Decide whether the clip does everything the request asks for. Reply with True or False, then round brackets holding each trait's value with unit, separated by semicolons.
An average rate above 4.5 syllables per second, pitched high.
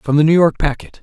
False (6.4 syllables/s; 155 Hz)